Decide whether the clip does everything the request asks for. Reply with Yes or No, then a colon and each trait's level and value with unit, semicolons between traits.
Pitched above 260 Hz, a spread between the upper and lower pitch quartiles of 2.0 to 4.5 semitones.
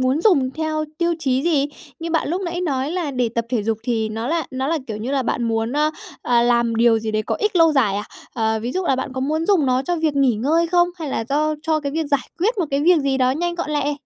No: very high, 280 Hz; average, 5.0 semitones